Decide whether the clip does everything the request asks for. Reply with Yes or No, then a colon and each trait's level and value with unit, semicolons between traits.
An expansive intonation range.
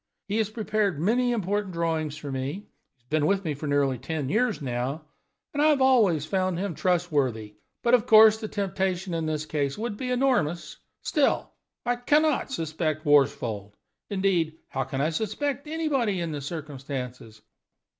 Yes: wide, 7.0 semitones